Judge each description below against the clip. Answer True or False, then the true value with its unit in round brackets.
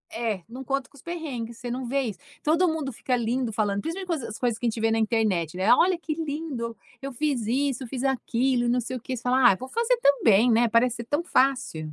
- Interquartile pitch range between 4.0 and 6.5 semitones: False (3.5 semitones)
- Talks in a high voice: True (250 Hz)